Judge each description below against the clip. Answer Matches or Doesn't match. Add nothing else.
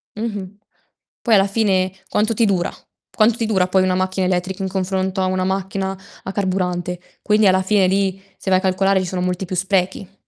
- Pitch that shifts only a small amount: Matches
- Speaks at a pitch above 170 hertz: Matches